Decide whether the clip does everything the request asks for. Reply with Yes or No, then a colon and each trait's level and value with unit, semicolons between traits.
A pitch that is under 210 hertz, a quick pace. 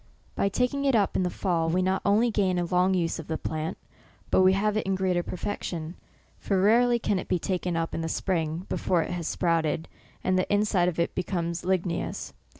Yes: medium, 185 Hz; fast, 215 wpm